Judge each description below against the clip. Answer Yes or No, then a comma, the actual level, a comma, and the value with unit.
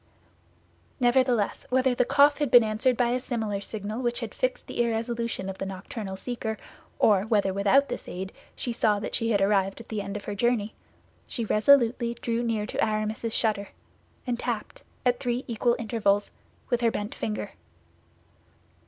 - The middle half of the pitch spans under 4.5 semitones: Yes, average, 2.8 semitones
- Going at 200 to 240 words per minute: No, average, 170 wpm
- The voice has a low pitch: No, high, 230 Hz